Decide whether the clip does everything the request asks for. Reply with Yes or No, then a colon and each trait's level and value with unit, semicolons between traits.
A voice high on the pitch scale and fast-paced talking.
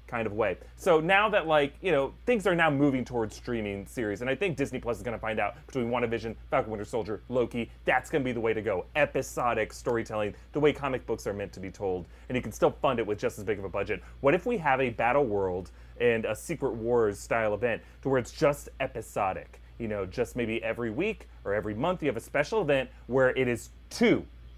No: low, 120 Hz; fast, 245 wpm